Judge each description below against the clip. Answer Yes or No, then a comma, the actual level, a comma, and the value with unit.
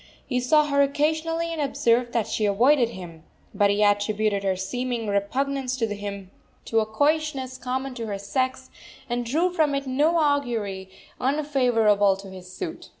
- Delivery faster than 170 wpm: No, average, 160 wpm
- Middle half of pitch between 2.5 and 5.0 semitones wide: No, wide, 5.6 semitones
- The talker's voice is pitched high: Yes, high, 245 Hz